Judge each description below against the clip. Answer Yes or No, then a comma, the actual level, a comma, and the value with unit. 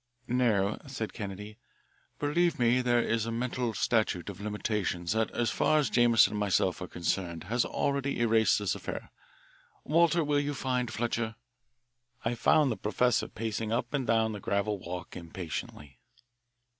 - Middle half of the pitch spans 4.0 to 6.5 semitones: No, average, 3.3 semitones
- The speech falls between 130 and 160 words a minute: Yes, average, 155 wpm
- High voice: No, low, 115 Hz